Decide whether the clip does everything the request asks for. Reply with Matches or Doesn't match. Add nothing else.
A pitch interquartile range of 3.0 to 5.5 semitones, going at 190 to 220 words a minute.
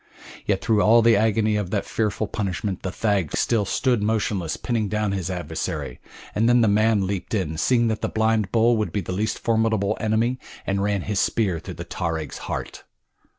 Doesn't match